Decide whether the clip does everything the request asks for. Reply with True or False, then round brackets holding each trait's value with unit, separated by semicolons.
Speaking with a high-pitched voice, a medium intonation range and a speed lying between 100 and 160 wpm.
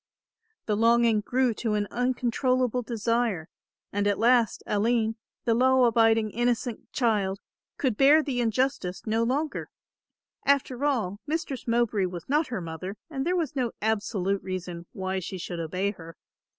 True (230 Hz; 4.1 semitones; 150 wpm)